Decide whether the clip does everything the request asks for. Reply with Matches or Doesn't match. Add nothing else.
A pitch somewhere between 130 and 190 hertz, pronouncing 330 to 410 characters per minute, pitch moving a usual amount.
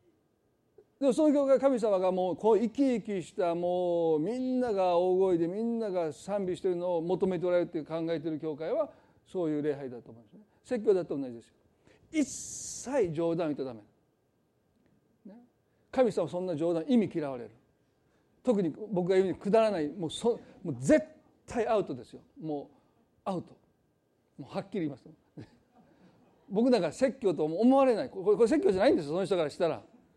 Doesn't match